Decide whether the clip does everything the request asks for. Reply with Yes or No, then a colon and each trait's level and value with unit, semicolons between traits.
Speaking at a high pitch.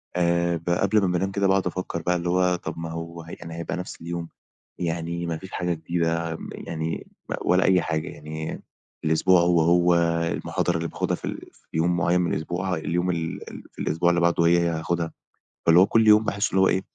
No: very low, 85 Hz